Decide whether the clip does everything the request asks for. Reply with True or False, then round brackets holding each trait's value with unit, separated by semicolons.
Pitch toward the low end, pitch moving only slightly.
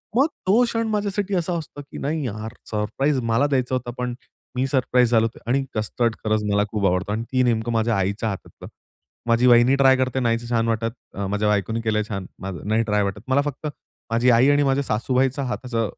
False (120 Hz; 3.7 semitones)